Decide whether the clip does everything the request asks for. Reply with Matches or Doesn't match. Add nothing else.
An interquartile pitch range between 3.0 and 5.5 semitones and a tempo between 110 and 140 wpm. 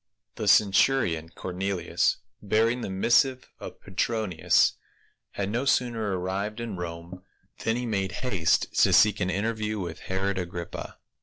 Matches